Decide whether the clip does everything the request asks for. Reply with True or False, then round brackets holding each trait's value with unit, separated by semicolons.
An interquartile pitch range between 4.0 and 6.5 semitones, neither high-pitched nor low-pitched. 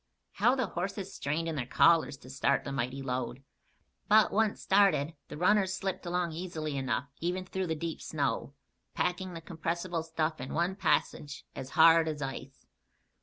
True (4.6 semitones; 165 Hz)